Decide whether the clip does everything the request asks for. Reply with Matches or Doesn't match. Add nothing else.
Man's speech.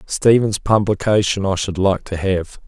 Matches